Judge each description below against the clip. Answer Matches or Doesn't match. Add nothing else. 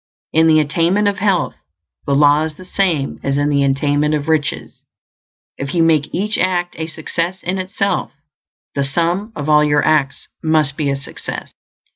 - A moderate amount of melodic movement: Matches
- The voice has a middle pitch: Matches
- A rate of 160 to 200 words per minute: Matches